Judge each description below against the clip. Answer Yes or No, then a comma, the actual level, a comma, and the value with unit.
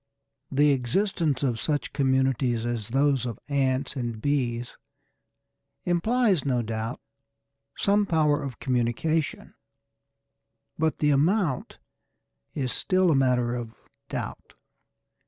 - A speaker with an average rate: No, slow, 105 wpm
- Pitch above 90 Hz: Yes, low, 135 Hz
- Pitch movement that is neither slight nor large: Yes, average, 4.3 semitones